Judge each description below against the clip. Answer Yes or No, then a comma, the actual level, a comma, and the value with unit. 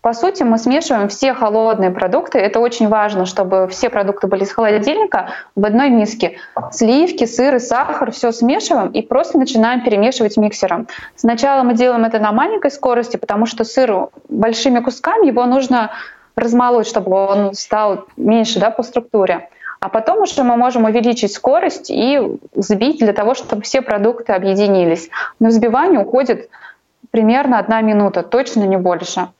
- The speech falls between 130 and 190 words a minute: Yes, average, 155 wpm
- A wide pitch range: No, average, 3.3 semitones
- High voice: Yes, high, 230 Hz